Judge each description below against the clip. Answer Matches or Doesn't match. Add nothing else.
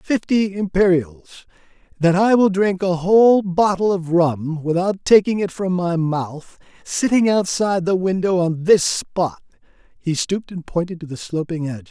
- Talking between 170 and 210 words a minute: Matches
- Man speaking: Matches